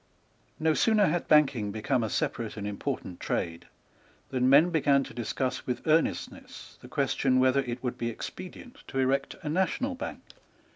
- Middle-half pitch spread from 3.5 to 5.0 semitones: Yes, average, 4.6 semitones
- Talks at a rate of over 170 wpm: No, average, 160 wpm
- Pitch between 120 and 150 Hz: Yes, low, 135 Hz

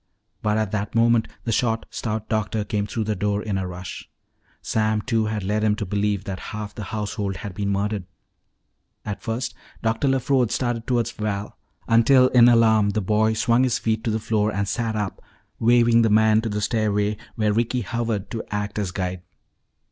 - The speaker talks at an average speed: Yes, average, 190 wpm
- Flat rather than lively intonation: Yes, narrow, 1.9 semitones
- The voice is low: Yes, low, 110 Hz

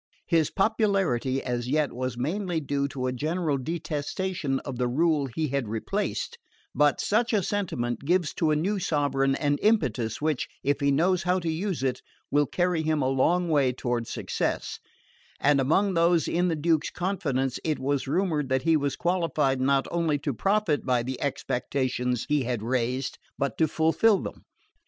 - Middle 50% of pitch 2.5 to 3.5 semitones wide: No, average, 4.6 semitones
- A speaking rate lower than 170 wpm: No, average, 175 wpm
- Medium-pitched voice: Yes, medium, 145 Hz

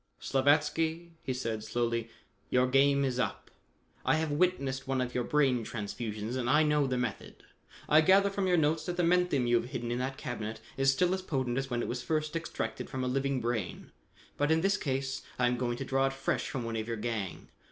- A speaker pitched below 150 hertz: Yes, low, 135 Hz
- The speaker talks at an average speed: No, fast, 220 wpm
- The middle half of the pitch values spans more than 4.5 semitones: No, average, 3.9 semitones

